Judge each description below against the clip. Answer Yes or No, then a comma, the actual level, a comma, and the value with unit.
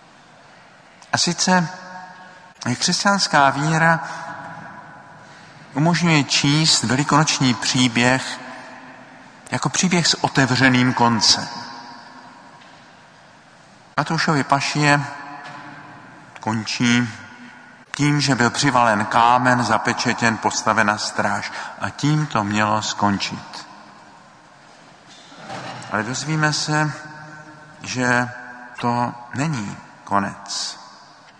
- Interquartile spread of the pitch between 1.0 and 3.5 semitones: No, average, 4.2 semitones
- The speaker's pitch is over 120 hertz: Yes, medium, 140 Hz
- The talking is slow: Yes, slow, 70 wpm